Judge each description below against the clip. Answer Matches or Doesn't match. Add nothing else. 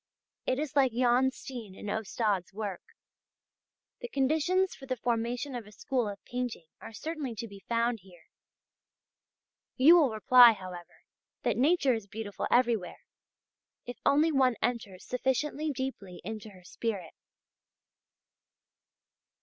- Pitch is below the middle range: Doesn't match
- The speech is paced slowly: Matches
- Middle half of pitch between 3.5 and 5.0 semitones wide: Matches